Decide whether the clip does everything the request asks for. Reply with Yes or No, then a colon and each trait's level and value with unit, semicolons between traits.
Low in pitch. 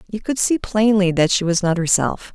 No: high, 195 Hz